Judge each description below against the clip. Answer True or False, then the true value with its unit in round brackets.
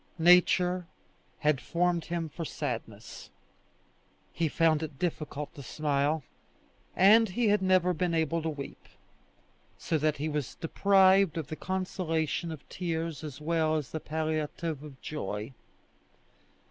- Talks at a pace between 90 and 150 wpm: True (135 wpm)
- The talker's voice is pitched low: False (160 Hz)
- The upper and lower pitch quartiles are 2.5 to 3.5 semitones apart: True (2.8 semitones)